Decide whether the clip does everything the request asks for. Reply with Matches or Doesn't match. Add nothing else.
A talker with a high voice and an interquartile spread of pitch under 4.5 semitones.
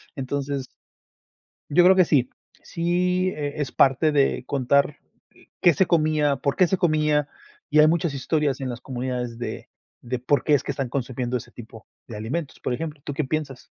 Doesn't match